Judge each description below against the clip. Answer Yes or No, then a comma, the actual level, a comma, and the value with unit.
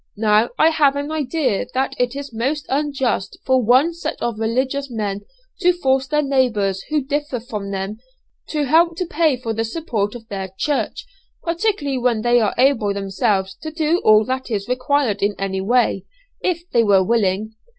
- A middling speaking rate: Yes, average, 180 wpm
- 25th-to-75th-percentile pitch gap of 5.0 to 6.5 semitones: Yes, wide, 5.5 semitones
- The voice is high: Yes, very high, 250 Hz